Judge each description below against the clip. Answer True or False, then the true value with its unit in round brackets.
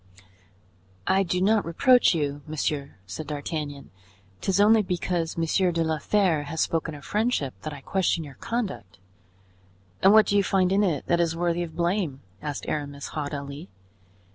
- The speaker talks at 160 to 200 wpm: True (165 wpm)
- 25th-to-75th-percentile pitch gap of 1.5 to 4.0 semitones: False (4.7 semitones)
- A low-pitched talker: False (165 Hz)